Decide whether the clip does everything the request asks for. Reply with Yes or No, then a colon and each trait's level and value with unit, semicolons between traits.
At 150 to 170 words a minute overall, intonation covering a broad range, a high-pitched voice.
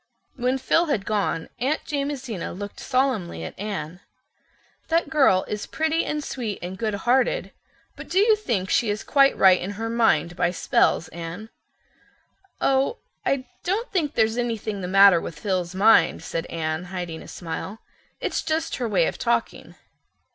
Yes: average, 160 wpm; wide, 6.9 semitones; high, 220 Hz